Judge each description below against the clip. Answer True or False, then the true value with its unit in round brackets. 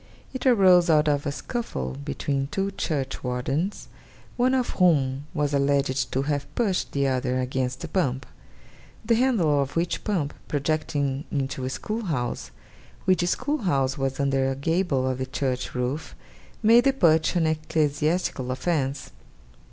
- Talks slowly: False (150 wpm)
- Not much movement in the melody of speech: False (4.9 semitones)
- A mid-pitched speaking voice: True (145 Hz)